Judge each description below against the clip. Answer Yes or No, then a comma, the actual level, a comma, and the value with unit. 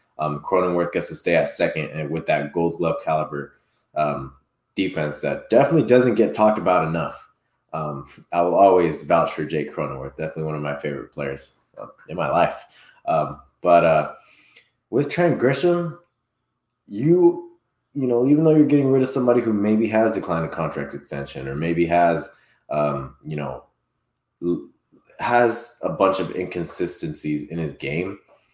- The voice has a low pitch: Yes, very low, 85 Hz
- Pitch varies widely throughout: Yes, wide, 8.7 semitones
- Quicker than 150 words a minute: Yes, average, 160 wpm